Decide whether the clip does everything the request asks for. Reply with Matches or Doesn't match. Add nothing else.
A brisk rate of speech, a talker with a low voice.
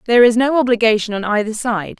Doesn't match